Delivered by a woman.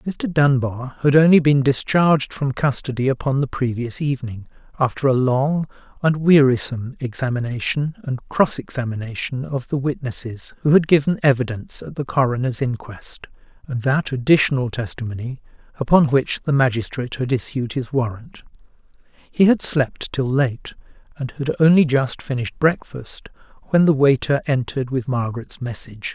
No: male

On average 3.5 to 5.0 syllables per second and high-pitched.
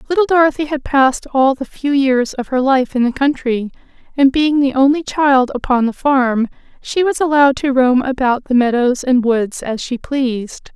Yes: 4.9 syllables/s; very high, 265 Hz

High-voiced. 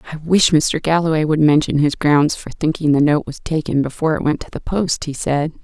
No: medium, 155 Hz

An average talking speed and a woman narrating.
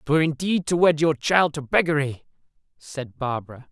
No: average, 160 wpm; male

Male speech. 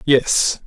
Yes: male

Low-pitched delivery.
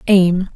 No: medium, 185 Hz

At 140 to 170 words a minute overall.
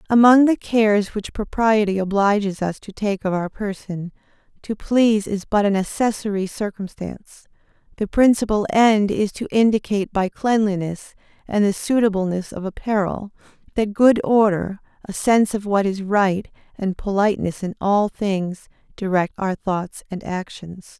Yes: average, 145 wpm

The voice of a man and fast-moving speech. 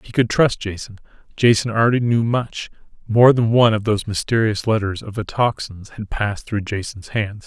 No: male; average, 175 wpm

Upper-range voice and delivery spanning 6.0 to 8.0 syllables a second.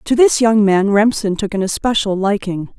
No: high, 210 Hz; 4.9 syllables/s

